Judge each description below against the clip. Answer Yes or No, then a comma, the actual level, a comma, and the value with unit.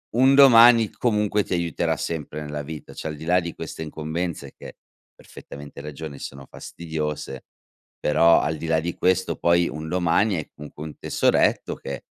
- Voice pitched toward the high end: No, very low, 80 Hz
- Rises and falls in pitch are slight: No, average, 3.3 semitones